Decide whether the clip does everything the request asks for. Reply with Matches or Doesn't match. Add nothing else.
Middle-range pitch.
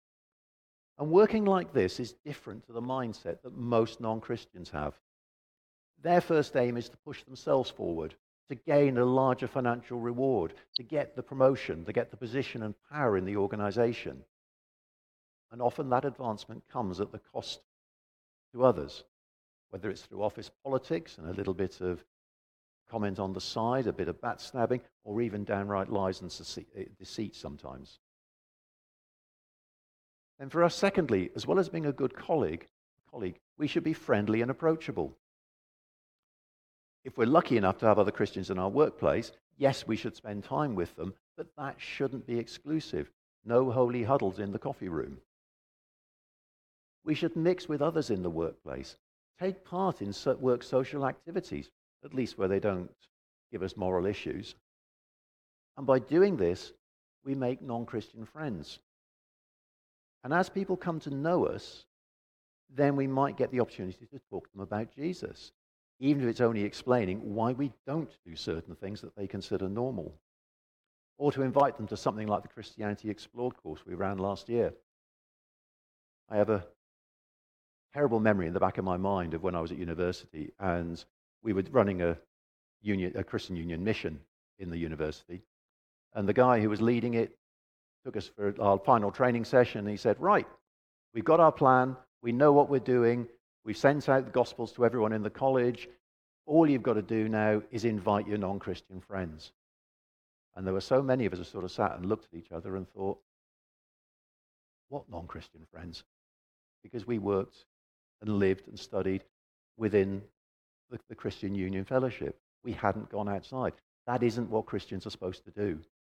Doesn't match